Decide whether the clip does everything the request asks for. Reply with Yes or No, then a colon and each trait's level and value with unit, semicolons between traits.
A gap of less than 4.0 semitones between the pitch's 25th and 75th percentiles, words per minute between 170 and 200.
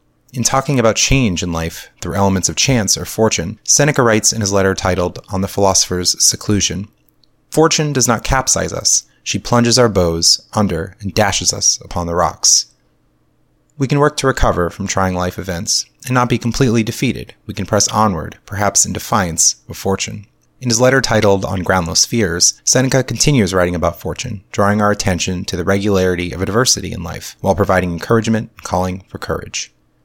No: average, 4.7 semitones; average, 180 wpm